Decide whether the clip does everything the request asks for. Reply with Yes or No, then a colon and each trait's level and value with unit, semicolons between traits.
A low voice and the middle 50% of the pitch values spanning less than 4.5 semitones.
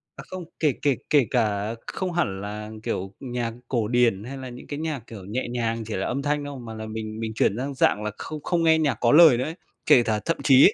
No: low, 120 Hz; average, 4.8 semitones